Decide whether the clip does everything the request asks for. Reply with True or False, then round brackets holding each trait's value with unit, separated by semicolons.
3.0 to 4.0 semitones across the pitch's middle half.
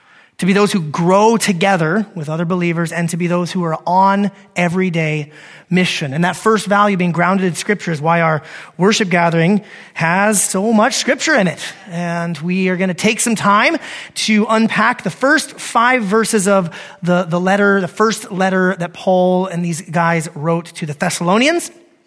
True (3.7 semitones)